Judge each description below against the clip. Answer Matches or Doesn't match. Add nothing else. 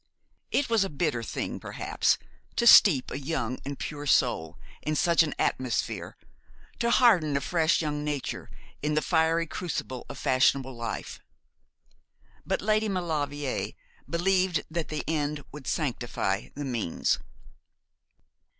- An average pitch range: Matches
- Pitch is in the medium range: Matches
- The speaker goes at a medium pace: Doesn't match